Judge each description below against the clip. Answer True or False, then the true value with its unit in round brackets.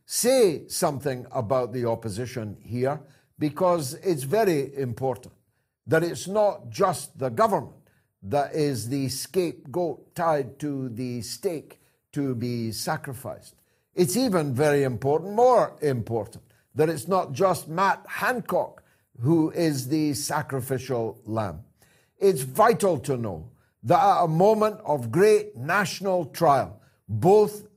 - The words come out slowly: True (125 wpm)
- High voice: False (145 Hz)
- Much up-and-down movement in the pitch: True (6.0 semitones)